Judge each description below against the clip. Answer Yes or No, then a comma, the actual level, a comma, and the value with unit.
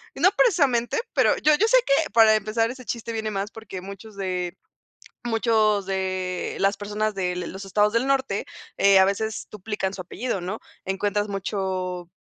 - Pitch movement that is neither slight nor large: Yes, average, 3.0 semitones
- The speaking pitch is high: Yes, high, 205 Hz